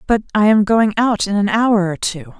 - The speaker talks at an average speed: No, fast, 250 wpm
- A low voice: No, high, 205 Hz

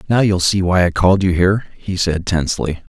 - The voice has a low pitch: Yes, very low, 90 Hz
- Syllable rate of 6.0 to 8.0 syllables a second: No, 5.8 syllables/s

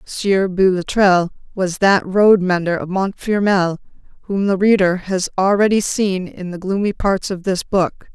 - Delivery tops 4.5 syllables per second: No, 4.3 syllables/s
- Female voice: Yes, female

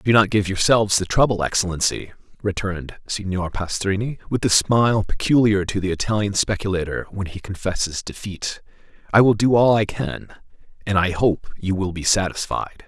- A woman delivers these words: No, male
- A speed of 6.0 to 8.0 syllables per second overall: No, 5.2 syllables/s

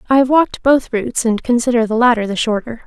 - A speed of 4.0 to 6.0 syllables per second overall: No, 6.4 syllables/s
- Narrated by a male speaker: No, female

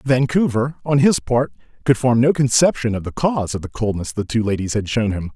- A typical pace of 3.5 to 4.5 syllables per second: No, 5.6 syllables/s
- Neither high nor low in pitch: No, low, 120 Hz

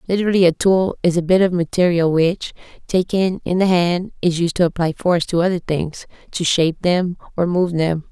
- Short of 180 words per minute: No, average, 200 wpm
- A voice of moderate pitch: Yes, medium, 175 Hz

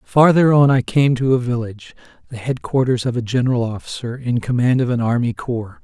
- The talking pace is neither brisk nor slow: Yes, average, 195 wpm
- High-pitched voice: No, low, 125 Hz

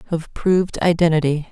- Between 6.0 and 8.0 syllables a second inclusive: No, 5.6 syllables/s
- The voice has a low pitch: No, medium, 165 Hz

